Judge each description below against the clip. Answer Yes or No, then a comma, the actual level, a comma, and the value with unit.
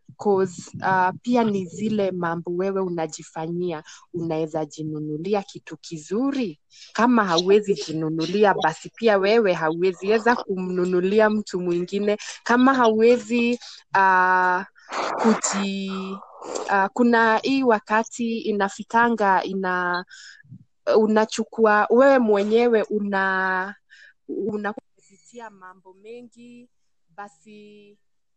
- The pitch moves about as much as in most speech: Yes, average, 3.4 semitones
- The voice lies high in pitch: Yes, high, 200 Hz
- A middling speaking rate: No, slow, 80 wpm